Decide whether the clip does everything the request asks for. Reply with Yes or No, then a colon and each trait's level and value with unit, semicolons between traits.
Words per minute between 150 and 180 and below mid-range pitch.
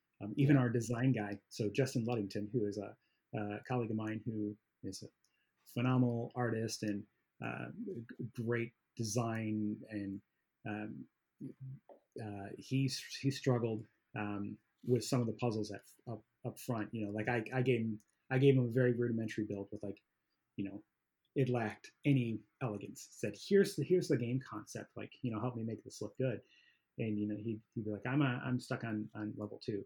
No: average, 190 wpm; low, 115 Hz